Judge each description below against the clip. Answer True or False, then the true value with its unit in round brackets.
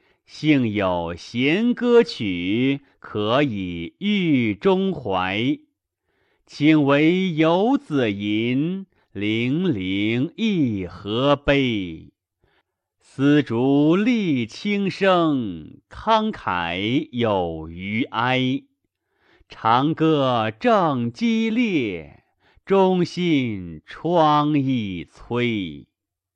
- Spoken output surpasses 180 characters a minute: False (90 characters per minute)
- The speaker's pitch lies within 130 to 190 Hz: True (140 Hz)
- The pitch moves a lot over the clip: True (8.8 semitones)